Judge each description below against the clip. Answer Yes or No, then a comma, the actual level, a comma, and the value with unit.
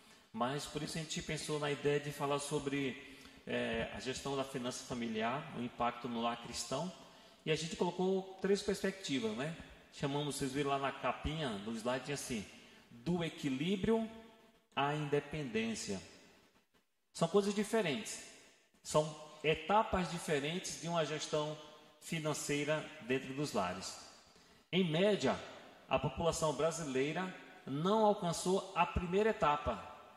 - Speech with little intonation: No, wide, 5.5 semitones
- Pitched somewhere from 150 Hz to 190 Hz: Yes, medium, 155 Hz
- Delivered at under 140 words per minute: Yes, average, 130 wpm